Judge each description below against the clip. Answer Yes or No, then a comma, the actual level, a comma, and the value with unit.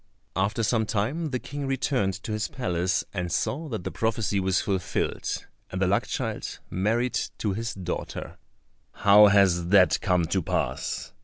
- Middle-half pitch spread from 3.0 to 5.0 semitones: Yes, average, 3.6 semitones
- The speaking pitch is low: Yes, low, 100 Hz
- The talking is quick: No, average, 160 wpm